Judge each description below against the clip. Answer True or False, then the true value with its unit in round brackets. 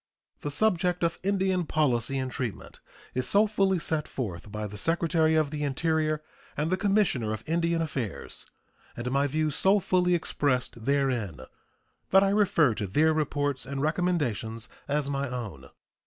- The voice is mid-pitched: True (150 Hz)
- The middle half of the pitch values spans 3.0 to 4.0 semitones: False (5.2 semitones)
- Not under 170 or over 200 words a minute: False (155 wpm)